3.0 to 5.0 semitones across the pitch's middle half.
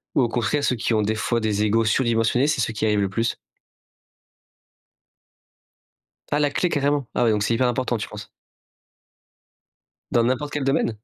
Yes: average, 3.9 semitones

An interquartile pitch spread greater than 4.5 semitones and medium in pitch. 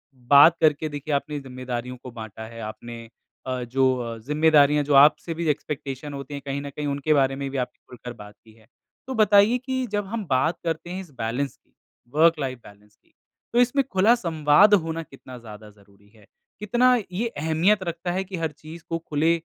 Yes: average, 5.0 semitones; medium, 145 Hz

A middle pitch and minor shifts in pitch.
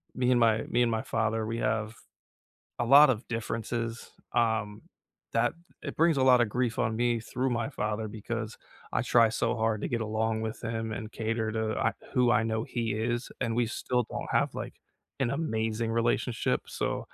No: low, 115 Hz; narrow, 1.5 semitones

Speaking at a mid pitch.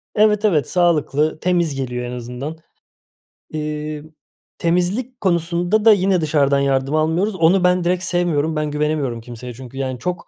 Yes: medium, 155 Hz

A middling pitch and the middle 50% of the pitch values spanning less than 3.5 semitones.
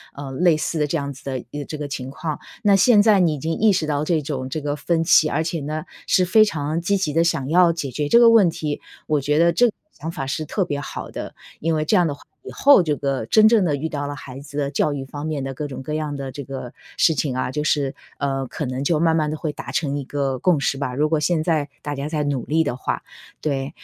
Yes: medium, 150 Hz; average, 2.8 semitones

